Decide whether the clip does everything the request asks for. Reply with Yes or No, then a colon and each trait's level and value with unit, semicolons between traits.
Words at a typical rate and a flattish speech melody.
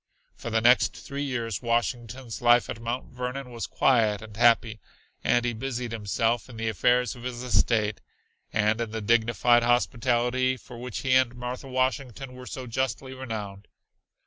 Yes: average, 165 wpm; narrow, 2.0 semitones